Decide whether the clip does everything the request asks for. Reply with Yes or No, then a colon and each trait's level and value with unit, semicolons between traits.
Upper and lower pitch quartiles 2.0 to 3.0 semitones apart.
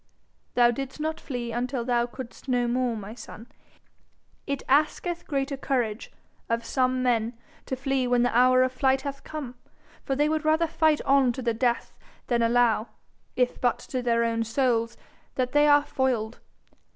Yes: narrow, 2.5 semitones